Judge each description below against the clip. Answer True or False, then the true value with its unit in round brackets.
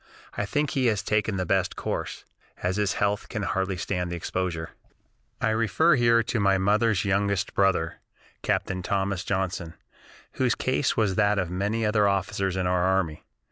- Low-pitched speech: True (100 Hz)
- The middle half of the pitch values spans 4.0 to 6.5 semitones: False (2.6 semitones)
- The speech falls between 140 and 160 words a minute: False (170 wpm)